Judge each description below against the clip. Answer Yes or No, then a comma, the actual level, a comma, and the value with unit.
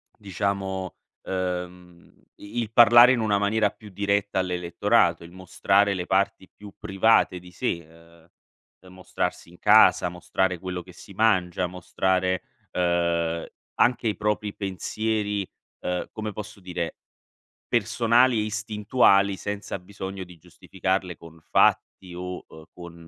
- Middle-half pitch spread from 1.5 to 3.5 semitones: Yes, average, 2.7 semitones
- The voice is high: No, very low, 95 Hz